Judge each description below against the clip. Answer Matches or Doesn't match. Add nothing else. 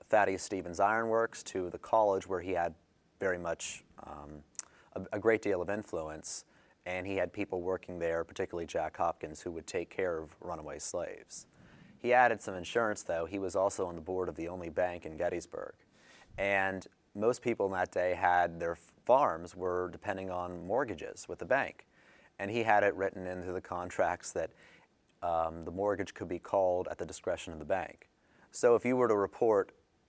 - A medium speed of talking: Matches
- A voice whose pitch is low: Matches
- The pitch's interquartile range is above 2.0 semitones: Matches